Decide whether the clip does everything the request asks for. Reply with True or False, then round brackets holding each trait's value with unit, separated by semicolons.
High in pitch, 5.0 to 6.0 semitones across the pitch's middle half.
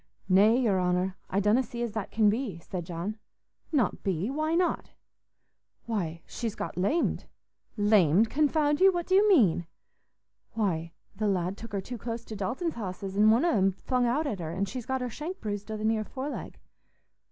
True (215 Hz; 5.3 semitones)